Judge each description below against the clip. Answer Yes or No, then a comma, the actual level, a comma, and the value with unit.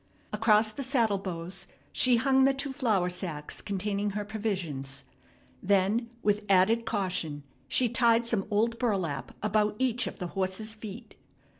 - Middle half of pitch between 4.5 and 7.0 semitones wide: No, average, 3.7 semitones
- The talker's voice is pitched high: Yes, high, 210 Hz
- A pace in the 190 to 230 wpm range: No, average, 145 wpm